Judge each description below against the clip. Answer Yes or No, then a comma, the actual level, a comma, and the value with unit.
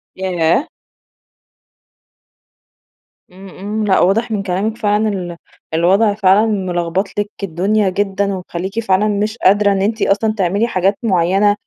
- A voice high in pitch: Yes, high, 195 Hz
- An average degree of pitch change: No, narrow, 2.2 semitones